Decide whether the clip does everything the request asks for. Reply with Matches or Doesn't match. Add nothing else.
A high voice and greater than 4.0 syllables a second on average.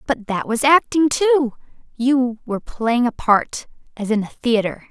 Matches